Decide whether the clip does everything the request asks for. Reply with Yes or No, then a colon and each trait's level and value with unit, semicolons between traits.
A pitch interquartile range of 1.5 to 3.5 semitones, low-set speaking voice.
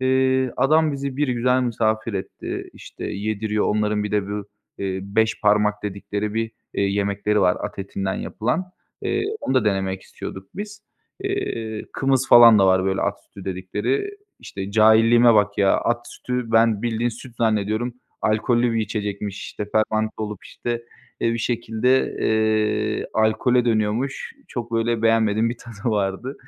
Yes: narrow, 2.6 semitones; low, 110 Hz